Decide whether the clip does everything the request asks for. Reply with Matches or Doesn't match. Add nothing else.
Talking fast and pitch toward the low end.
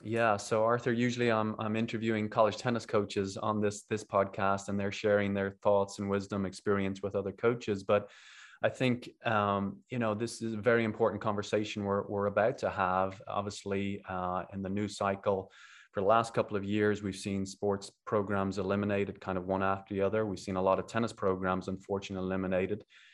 Doesn't match